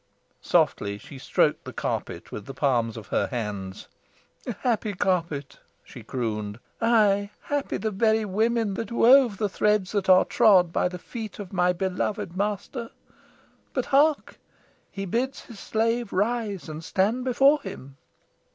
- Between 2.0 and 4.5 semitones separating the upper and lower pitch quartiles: No, wide, 5.4 semitones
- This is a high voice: Yes, high, 200 Hz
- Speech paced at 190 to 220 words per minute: No, average, 145 wpm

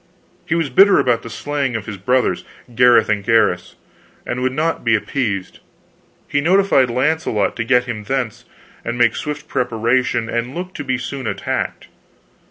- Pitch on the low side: Yes, low, 125 Hz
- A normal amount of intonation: Yes, average, 3.5 semitones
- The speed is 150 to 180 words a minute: Yes, average, 165 wpm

